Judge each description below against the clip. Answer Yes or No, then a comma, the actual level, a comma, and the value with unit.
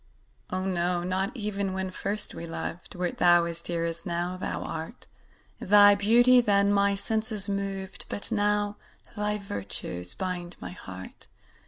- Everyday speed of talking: Yes, average, 150 wpm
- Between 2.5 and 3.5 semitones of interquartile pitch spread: Yes, average, 2.9 semitones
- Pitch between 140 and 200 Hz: Yes, high, 190 Hz